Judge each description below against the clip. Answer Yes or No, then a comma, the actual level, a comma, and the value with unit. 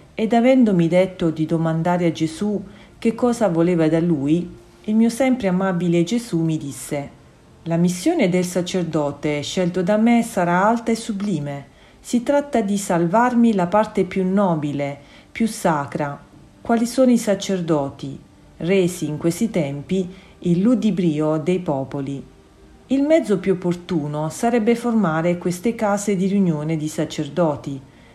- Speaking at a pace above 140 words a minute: No, average, 135 wpm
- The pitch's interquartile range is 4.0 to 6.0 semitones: Yes, average, 5.2 semitones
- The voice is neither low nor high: Yes, medium, 180 Hz